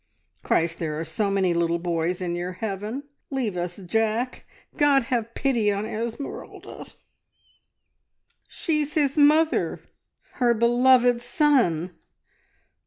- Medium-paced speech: No, slow, 110 wpm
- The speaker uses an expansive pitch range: Yes, wide, 6.6 semitones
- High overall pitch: Yes, high, 225 Hz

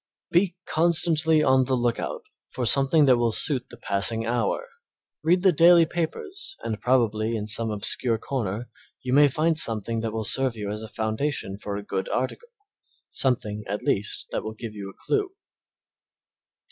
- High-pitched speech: No, low, 120 Hz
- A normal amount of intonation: No, wide, 6.0 semitones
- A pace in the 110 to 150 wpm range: No, average, 170 wpm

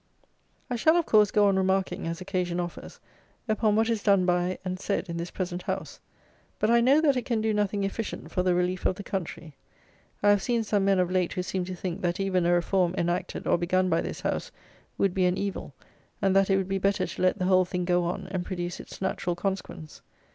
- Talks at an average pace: No, fast, 235 wpm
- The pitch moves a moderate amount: No, narrow, 2.2 semitones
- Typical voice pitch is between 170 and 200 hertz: Yes, medium, 185 Hz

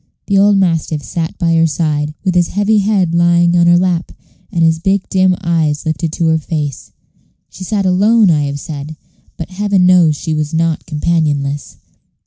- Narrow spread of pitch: No, average, 3.0 semitones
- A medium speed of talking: Yes, average, 180 wpm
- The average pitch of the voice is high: No, medium, 170 Hz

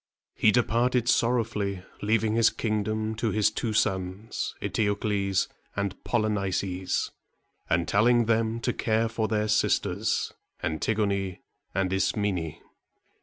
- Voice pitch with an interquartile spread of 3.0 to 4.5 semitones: No, narrow, 2.4 semitones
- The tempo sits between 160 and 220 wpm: No, average, 140 wpm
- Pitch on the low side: Yes, low, 105 Hz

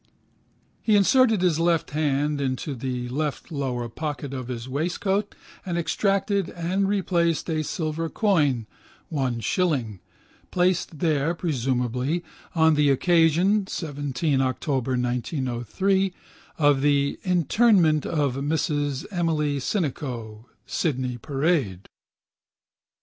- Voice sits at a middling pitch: Yes, medium, 150 Hz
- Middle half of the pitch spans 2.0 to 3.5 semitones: No, average, 4.8 semitones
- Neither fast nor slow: No, slow, 105 wpm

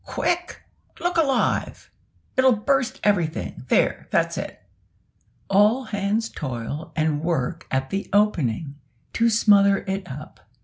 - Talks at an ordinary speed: No, slow, 120 wpm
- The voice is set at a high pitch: Yes, high, 200 Hz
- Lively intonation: Yes, wide, 6.8 semitones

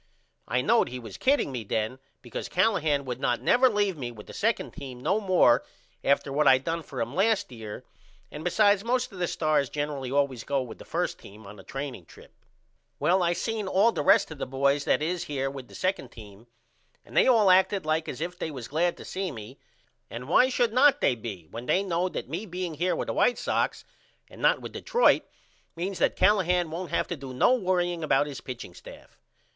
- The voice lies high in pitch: No, medium, 155 Hz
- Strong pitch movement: Yes, wide, 6.6 semitones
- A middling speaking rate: No, fast, 220 wpm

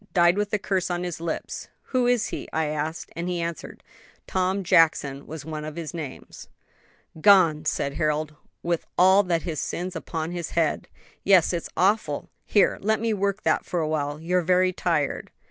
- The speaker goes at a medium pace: Yes, average, 180 wpm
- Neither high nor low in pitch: Yes, medium, 170 Hz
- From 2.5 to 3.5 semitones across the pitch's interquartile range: Yes, average, 3.1 semitones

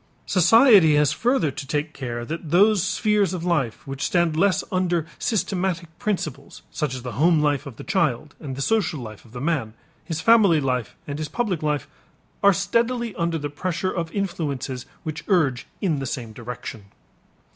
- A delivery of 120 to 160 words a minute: No, average, 180 wpm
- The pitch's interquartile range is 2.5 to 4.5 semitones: No, average, 5.3 semitones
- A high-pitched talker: No, medium, 160 Hz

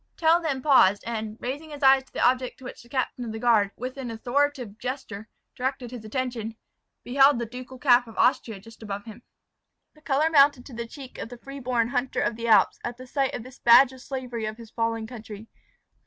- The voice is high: Yes, high, 245 Hz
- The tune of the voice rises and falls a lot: No, average, 2.8 semitones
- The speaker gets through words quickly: Yes, fast, 220 wpm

